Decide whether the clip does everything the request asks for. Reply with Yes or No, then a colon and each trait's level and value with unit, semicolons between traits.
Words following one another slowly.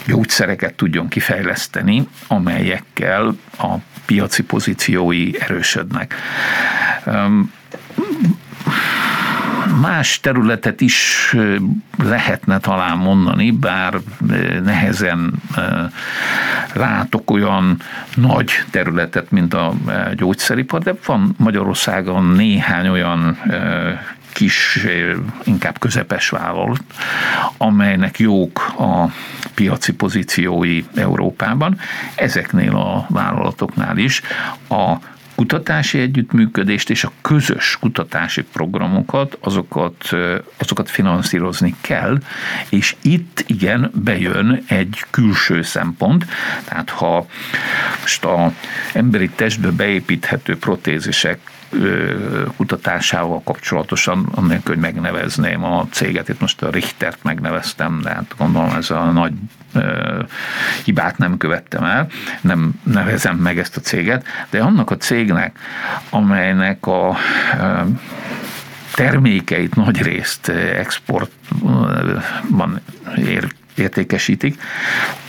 Yes: slow, 85 wpm